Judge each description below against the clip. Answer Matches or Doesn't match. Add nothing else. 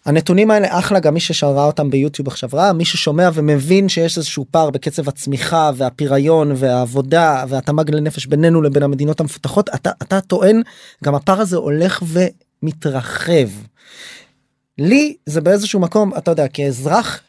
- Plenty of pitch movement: Doesn't match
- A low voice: Doesn't match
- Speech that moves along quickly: Doesn't match